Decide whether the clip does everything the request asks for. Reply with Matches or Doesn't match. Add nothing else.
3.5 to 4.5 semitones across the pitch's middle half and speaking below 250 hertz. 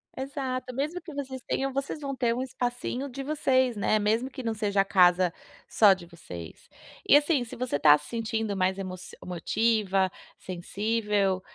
Doesn't match